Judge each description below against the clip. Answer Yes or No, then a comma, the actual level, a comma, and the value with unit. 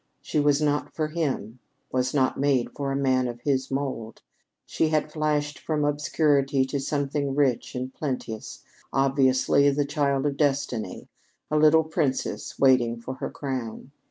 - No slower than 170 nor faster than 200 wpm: No, average, 155 wpm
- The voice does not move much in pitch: Yes, narrow, 2.1 semitones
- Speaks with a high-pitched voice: No, medium, 140 Hz